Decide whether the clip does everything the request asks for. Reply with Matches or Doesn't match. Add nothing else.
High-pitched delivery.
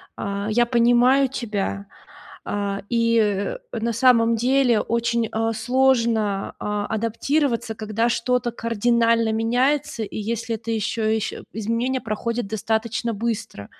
Matches